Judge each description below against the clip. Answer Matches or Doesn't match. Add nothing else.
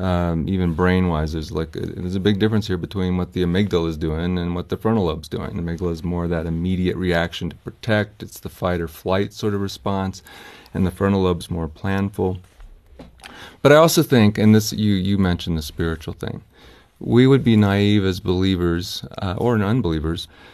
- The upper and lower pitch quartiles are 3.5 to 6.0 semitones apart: Doesn't match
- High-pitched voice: Doesn't match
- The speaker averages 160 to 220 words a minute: Matches